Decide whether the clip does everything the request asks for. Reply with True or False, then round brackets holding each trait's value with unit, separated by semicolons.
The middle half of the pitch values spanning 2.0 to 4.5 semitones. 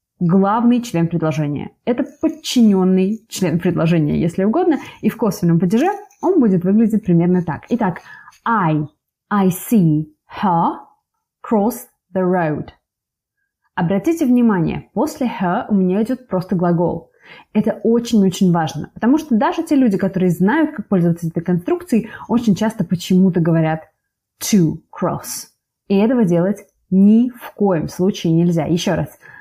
False (5.2 semitones)